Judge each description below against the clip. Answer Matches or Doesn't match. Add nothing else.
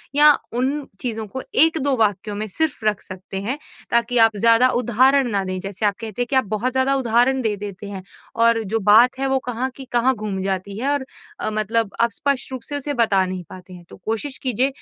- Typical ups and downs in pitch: Matches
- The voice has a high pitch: Matches